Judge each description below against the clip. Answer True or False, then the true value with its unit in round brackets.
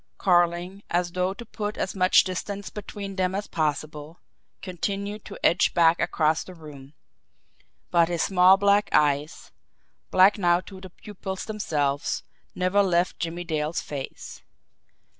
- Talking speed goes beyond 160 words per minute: False (140 wpm)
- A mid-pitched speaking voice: True (180 Hz)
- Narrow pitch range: False (3.2 semitones)